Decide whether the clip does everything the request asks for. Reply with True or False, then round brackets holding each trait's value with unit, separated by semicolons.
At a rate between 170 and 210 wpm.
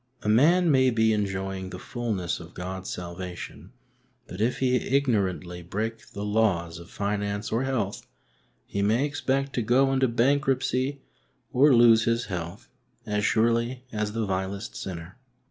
False (145 wpm)